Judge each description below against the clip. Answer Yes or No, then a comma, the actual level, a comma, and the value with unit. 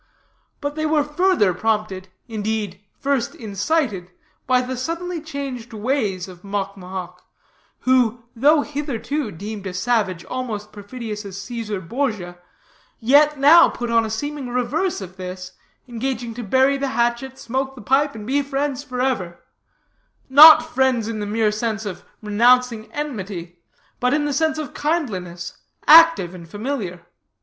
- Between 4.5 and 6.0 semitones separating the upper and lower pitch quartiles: Yes, wide, 5.4 semitones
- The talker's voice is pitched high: Yes, high, 235 Hz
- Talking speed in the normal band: Yes, average, 145 wpm